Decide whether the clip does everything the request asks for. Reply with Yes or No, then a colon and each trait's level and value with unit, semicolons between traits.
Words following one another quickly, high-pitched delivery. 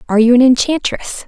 No: average, 190 wpm; very high, 250 Hz